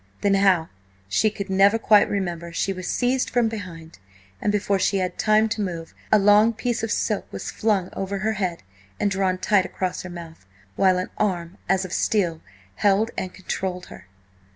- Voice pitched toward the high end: Yes, high, 195 Hz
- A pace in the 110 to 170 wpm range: No, average, 185 wpm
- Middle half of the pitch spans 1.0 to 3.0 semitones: Yes, narrow, 2.6 semitones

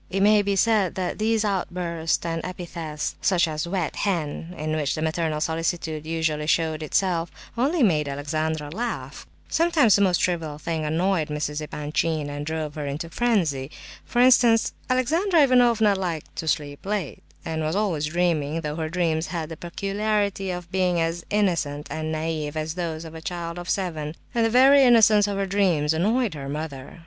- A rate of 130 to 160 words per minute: No, average, 175 wpm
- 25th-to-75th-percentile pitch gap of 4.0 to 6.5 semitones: Yes, average, 4.3 semitones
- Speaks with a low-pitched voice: No, medium, 170 Hz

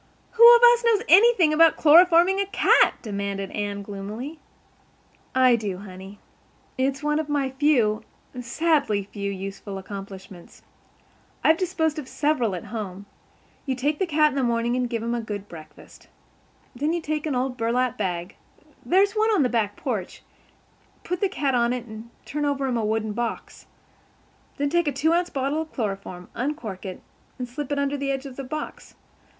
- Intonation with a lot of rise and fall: Yes, wide, 6.5 semitones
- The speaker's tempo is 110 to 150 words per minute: No, average, 170 wpm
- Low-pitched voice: No, very high, 255 Hz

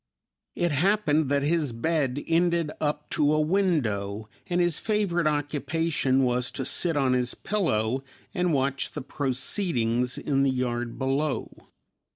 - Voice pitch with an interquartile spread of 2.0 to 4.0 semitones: No, average, 4.6 semitones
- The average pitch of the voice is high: No, medium, 145 Hz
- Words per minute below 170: Yes, average, 140 wpm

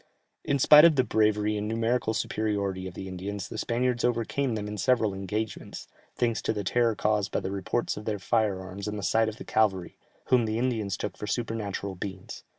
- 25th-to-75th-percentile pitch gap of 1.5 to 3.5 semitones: Yes, average, 2.8 semitones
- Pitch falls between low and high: No, low, 105 Hz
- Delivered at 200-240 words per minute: Yes, fast, 205 wpm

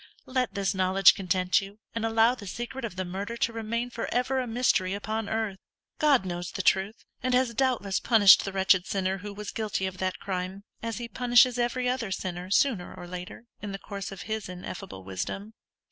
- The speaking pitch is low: No, high, 205 Hz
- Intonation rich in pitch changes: No, average, 3.7 semitones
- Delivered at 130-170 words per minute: No, average, 200 wpm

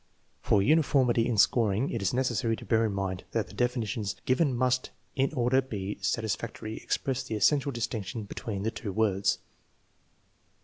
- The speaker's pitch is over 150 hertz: No, low, 115 Hz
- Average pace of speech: Yes, average, 165 wpm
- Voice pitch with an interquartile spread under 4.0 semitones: Yes, average, 3.6 semitones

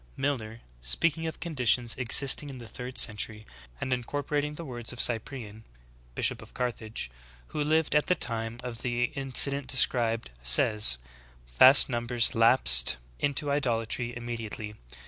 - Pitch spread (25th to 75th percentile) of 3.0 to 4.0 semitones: Yes, average, 3.6 semitones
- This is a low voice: Yes, low, 120 Hz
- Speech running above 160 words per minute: No, average, 145 wpm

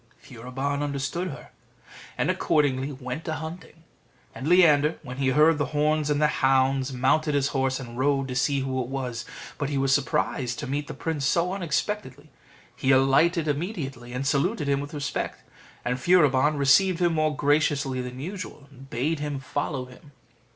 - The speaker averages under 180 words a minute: Yes, average, 170 wpm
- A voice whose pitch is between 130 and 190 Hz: Yes, medium, 140 Hz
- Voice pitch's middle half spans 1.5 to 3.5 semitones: Yes, narrow, 2.6 semitones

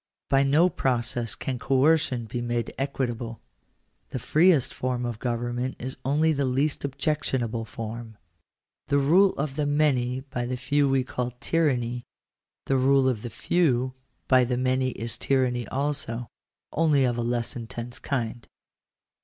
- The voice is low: Yes, low, 130 Hz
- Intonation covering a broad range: No, narrow, 2.6 semitones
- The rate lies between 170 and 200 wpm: No, average, 145 wpm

